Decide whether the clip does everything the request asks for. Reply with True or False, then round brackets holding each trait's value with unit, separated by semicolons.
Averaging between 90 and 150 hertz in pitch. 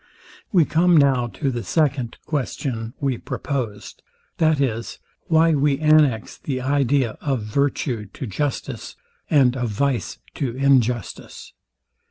True (135 Hz)